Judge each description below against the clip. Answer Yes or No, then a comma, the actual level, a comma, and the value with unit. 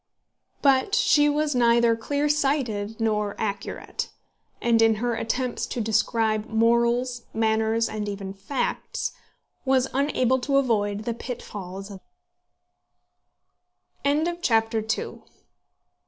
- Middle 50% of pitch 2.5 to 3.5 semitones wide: Yes, average, 3.2 semitones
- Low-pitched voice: No, high, 230 Hz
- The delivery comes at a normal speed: No, slow, 100 wpm